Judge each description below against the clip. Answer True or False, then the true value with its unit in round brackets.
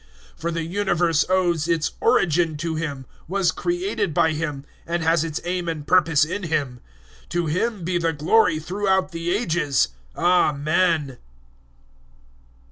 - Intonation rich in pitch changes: False (2.7 semitones)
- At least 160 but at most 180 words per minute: False (140 wpm)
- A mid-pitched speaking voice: True (165 Hz)